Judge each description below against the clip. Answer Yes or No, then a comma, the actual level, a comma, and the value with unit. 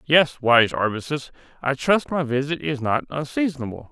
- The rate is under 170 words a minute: Yes, average, 140 wpm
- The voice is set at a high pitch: No, medium, 140 Hz